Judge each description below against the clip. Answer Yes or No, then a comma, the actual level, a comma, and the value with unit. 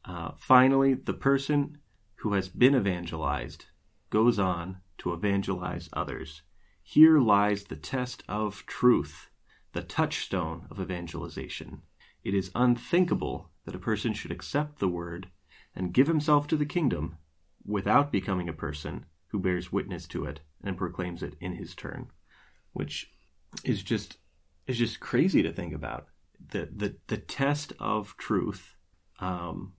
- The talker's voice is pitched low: Yes, very low, 95 Hz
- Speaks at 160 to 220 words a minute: No, average, 140 wpm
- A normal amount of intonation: No, wide, 6.3 semitones